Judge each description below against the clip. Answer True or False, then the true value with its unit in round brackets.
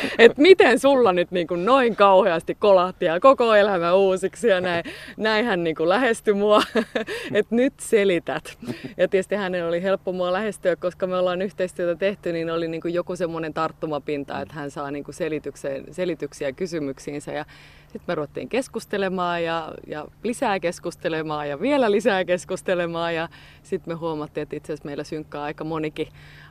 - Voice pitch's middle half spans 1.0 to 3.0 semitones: False (4.1 semitones)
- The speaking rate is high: True (160 wpm)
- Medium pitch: True (180 Hz)